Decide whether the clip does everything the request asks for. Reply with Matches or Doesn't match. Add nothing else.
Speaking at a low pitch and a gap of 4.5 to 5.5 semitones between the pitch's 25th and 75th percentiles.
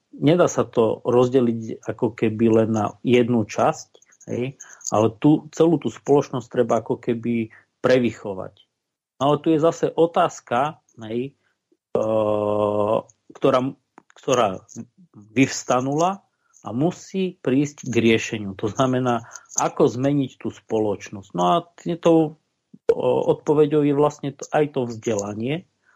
Matches